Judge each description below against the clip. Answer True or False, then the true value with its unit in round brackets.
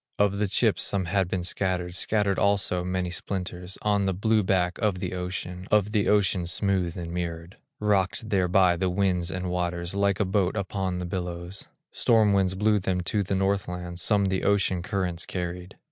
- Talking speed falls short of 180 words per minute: False (185 wpm)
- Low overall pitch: True (95 Hz)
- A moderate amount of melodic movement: False (2.0 semitones)